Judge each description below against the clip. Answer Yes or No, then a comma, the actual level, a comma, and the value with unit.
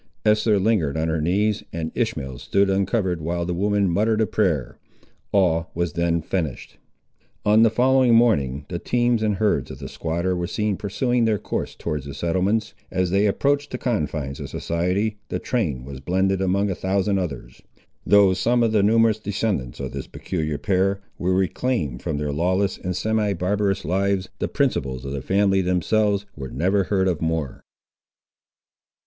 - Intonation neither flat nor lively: Yes, average, 4.2 semitones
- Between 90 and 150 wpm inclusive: No, average, 170 wpm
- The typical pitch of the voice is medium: No, very low, 95 Hz